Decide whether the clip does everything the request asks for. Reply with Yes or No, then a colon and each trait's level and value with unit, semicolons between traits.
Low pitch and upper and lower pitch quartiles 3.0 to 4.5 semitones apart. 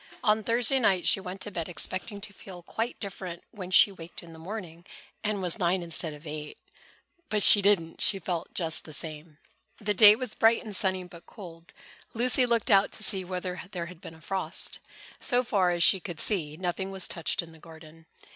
No: medium, 185 Hz; average, 3.6 semitones